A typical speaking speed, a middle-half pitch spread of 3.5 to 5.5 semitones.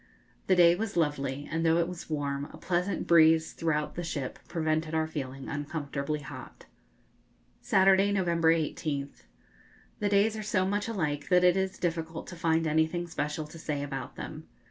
No: average, 165 wpm; average, 3.1 semitones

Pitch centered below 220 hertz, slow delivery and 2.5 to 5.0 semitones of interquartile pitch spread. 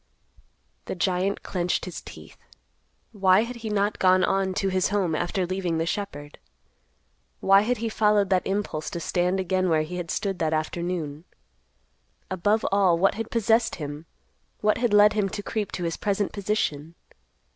No: high, 190 Hz; average, 165 wpm; average, 3.1 semitones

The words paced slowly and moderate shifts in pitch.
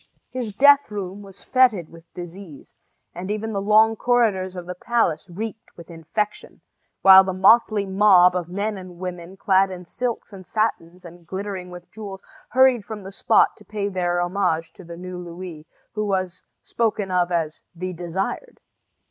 No: average, 170 wpm; average, 3.0 semitones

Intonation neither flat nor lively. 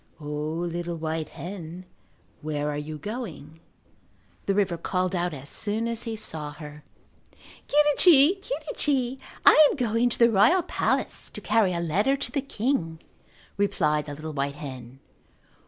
No: wide, 7.3 semitones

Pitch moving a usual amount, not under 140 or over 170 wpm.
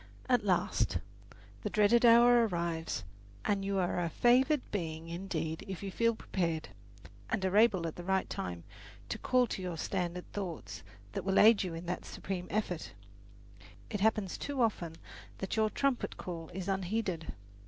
Yes: average, 4.2 semitones; average, 165 wpm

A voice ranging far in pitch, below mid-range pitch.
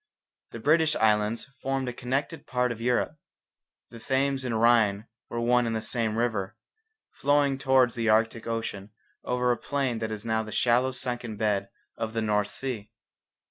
No: average, 2.9 semitones; low, 120 Hz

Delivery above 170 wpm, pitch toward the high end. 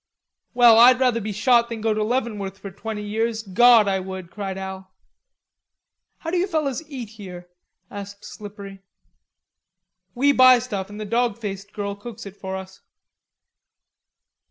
No: average, 155 wpm; high, 210 Hz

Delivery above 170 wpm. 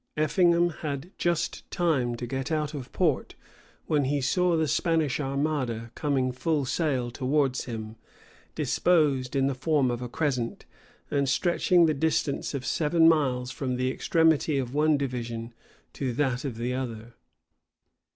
No: average, 150 wpm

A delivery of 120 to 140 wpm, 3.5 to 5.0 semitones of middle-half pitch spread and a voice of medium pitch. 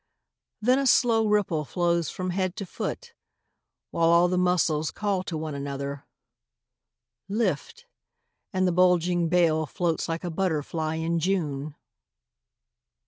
No: slow, 135 wpm; average, 2.8 semitones; medium, 175 Hz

